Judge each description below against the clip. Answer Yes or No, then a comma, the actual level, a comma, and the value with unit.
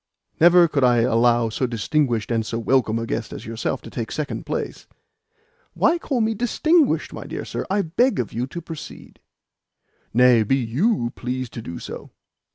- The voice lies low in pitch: Yes, low, 125 Hz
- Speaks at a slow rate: No, average, 175 wpm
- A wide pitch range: Yes, wide, 6.9 semitones